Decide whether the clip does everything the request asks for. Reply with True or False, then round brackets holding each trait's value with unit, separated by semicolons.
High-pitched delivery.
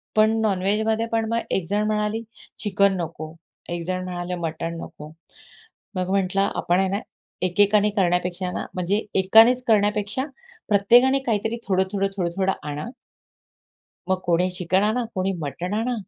True (195 Hz)